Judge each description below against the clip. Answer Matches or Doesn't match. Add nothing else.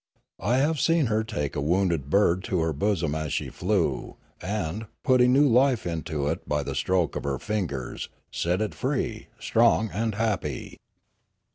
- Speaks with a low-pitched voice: Matches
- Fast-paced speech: Doesn't match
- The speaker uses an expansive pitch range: Matches